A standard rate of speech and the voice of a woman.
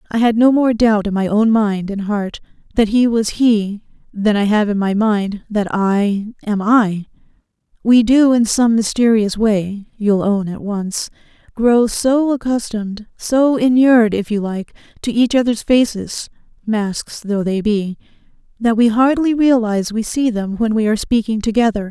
Yes: average, 170 wpm; female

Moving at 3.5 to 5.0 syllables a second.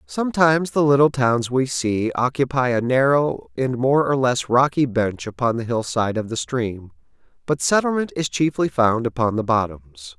Yes: 4.7 syllables/s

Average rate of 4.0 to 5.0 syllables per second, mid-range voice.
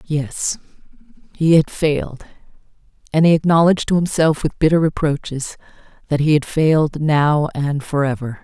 Yes: 4.9 syllables/s; medium, 150 Hz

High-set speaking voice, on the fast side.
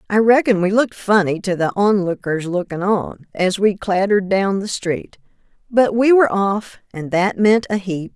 No: high, 200 Hz; average, 185 wpm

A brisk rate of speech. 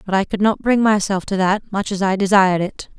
Yes: fast, 260 wpm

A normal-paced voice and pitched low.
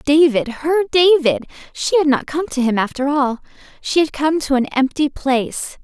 No: average, 165 wpm; very high, 285 Hz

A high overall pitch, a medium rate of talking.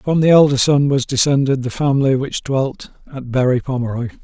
No: low, 135 Hz; average, 185 wpm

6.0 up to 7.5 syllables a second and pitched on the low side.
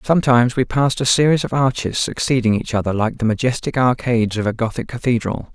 Yes: 6.2 syllables/s; low, 120 Hz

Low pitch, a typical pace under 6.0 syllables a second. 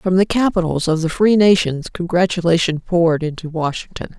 No: medium, 175 Hz; 5.4 syllables/s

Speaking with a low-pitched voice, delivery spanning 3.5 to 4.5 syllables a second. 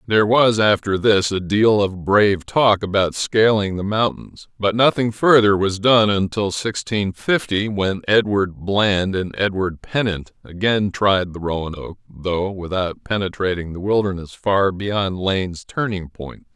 Yes: low, 100 Hz; 4.3 syllables/s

